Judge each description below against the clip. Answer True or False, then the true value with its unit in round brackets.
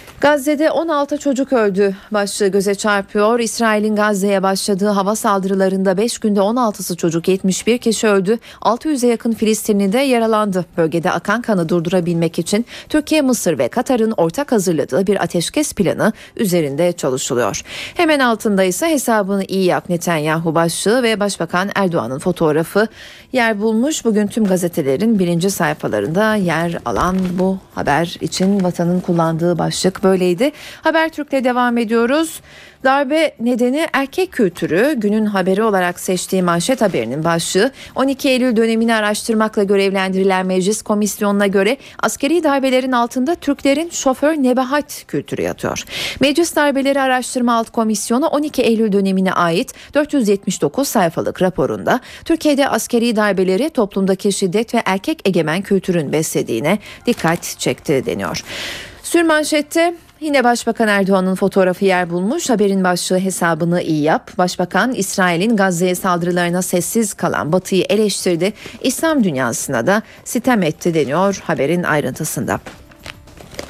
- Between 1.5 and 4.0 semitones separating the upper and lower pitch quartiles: False (5.0 semitones)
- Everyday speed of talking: True (125 wpm)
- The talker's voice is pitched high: True (205 Hz)